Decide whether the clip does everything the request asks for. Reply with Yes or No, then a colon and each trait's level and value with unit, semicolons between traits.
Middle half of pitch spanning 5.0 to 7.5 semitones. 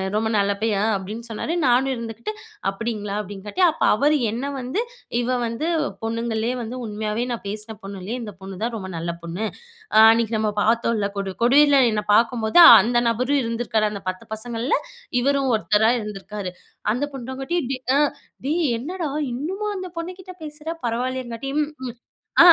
No: average, 4.0 semitones